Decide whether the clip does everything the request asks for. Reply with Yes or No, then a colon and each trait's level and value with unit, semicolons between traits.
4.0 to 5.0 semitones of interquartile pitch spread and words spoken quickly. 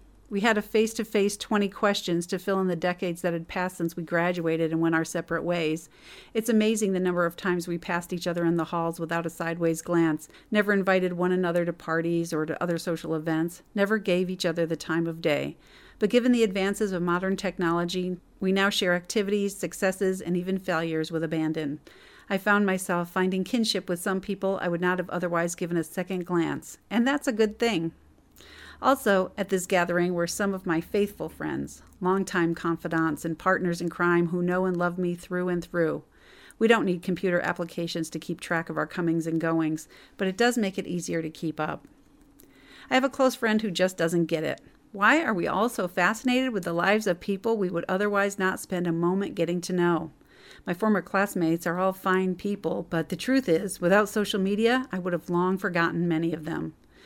No: average, 3.0 semitones; fast, 210 wpm